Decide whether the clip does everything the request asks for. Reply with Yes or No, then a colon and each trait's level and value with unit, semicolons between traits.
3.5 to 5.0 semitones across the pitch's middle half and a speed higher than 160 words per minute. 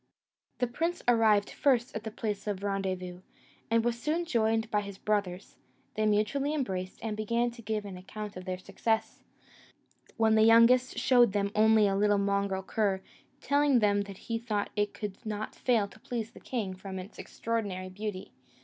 No: narrow, 2.6 semitones; average, 175 wpm